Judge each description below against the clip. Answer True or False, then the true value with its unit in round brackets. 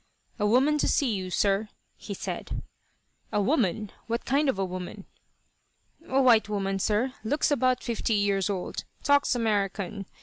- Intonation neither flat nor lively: True (4.5 semitones)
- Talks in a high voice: True (215 Hz)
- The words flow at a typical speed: True (155 wpm)